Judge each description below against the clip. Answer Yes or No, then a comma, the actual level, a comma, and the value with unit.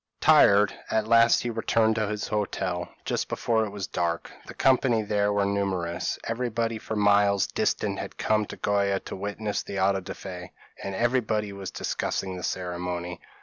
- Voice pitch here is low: Yes, low, 100 Hz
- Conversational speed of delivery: Yes, average, 175 wpm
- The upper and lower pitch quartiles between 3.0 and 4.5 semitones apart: No, narrow, 2.5 semitones